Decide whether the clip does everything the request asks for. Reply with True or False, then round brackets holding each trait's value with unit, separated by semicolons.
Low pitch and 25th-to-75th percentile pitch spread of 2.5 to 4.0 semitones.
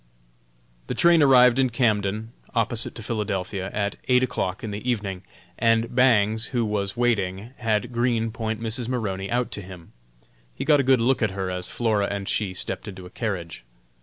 True (110 Hz; 3.5 semitones)